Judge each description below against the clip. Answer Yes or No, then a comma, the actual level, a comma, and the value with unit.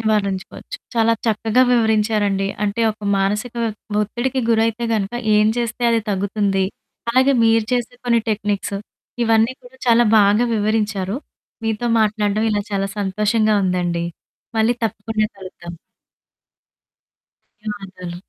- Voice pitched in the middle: No, high, 215 Hz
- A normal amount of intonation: No, narrow, 2.2 semitones